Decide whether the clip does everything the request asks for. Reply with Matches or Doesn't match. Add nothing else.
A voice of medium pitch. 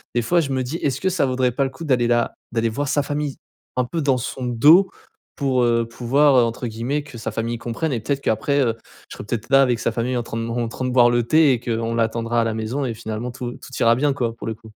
Doesn't match